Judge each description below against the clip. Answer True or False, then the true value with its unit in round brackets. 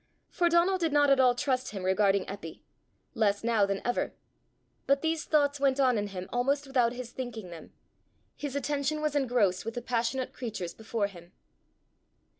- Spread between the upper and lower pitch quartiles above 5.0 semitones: True (5.5 semitones)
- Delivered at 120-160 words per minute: False (175 wpm)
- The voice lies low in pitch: False (245 Hz)